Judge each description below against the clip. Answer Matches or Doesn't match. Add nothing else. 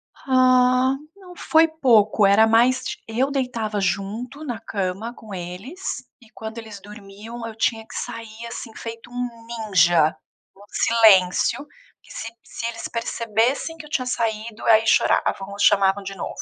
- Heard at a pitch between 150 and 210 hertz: Doesn't match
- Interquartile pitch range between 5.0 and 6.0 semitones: Doesn't match